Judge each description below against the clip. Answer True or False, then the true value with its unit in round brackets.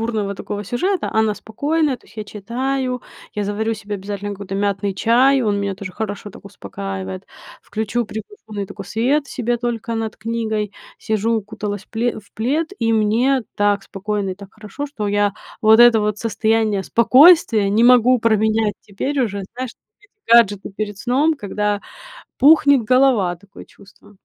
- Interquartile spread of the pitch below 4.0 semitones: True (2.9 semitones)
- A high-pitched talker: True (220 Hz)